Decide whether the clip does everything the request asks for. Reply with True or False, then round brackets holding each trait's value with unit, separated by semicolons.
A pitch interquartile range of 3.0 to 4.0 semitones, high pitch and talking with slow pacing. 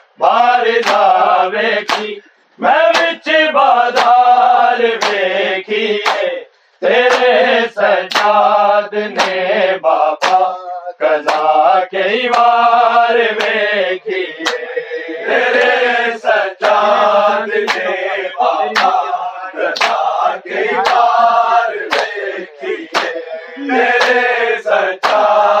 True (3.5 semitones; 230 Hz; 35 wpm)